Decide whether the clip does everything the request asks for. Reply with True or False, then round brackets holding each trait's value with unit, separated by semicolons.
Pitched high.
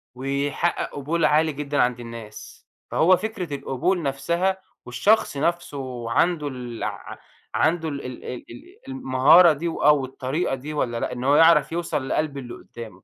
False (145 Hz)